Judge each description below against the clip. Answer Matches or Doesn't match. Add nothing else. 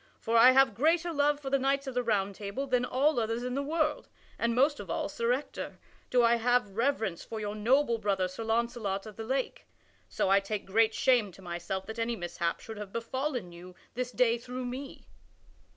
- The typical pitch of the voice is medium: Doesn't match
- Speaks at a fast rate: Matches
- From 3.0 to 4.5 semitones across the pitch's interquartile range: Matches